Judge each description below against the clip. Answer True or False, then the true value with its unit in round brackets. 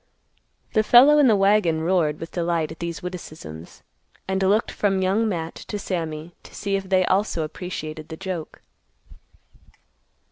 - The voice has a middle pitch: True (180 Hz)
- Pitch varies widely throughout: False (3.5 semitones)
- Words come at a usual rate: True (150 wpm)